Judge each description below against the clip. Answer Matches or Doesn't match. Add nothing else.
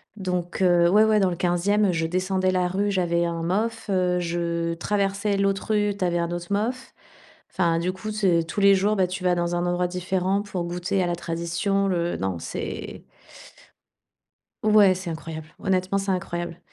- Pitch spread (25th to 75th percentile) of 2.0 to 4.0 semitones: Matches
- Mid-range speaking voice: Matches